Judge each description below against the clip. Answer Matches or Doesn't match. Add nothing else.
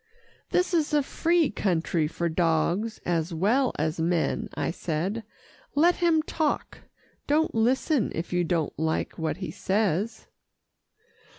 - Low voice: Doesn't match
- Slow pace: Matches